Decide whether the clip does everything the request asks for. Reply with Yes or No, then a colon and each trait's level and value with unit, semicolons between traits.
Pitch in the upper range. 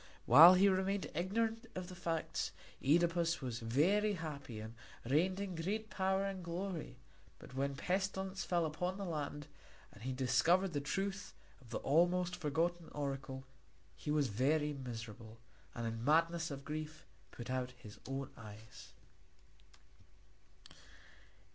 No: medium, 160 Hz